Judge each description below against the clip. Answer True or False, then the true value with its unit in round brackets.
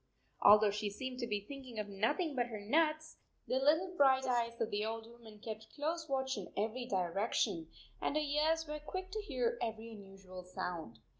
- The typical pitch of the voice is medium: False (235 Hz)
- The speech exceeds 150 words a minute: True (190 wpm)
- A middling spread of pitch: False (6.1 semitones)